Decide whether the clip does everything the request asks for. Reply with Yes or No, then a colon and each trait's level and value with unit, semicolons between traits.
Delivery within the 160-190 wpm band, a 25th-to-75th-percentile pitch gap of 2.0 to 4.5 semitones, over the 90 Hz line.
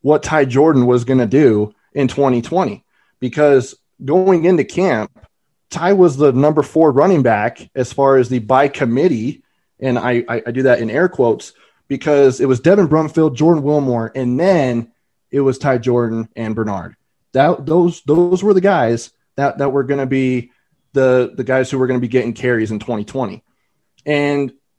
Yes: average, 180 wpm; average, 3.3 semitones; low, 135 Hz